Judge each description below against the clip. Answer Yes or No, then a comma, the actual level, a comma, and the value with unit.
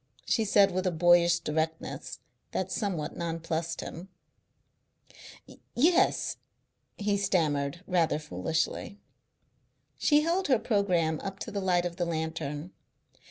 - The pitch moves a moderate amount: Yes, average, 3.8 semitones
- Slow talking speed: Yes, slow, 115 wpm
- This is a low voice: No, medium, 175 Hz